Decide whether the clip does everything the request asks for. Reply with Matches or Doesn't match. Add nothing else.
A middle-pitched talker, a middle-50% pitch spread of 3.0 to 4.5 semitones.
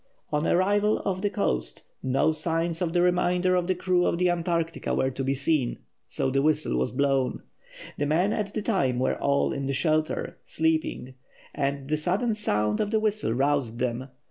Doesn't match